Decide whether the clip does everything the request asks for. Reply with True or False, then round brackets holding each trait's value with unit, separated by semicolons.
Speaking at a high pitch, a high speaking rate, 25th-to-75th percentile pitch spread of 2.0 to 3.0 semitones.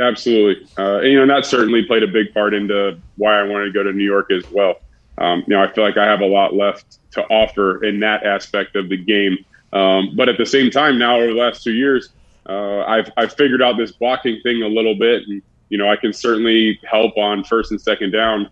False (105 Hz; 245 wpm; 2.6 semitones)